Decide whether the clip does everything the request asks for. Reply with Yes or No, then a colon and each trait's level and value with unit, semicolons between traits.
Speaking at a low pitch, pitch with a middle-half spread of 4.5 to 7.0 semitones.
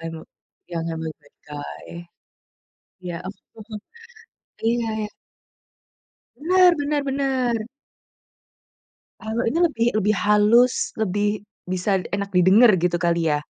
No: high, 210 Hz; average, 4.9 semitones